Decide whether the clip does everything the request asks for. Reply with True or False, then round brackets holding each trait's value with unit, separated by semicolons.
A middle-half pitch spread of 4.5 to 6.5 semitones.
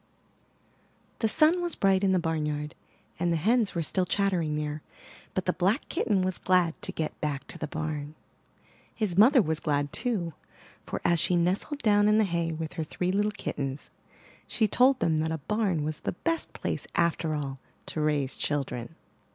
True (5.1 semitones)